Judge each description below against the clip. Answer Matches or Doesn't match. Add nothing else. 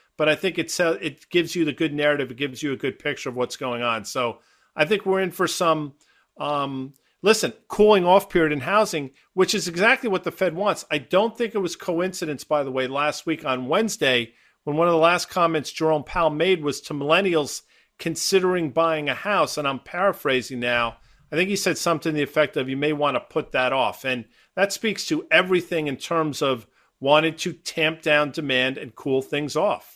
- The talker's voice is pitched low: Doesn't match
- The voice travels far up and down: Doesn't match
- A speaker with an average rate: Doesn't match